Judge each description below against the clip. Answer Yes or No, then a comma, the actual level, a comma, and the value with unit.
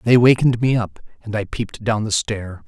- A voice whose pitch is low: Yes, low, 110 Hz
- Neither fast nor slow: No, fast, 225 wpm